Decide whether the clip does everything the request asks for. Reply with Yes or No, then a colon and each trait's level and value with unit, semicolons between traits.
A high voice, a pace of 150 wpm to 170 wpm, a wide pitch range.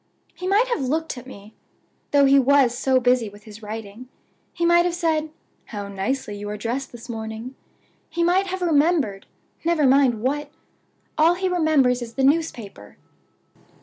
Yes: very high, 265 Hz; average, 165 wpm; wide, 6.4 semitones